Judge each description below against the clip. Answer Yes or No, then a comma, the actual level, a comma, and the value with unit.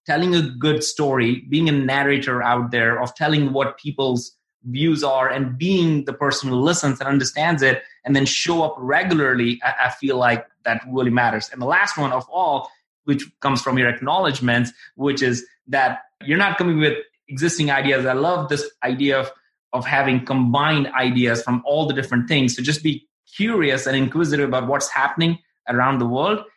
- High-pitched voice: No, medium, 140 Hz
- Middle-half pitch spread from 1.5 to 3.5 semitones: Yes, average, 3.0 semitones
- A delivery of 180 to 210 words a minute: Yes, average, 185 wpm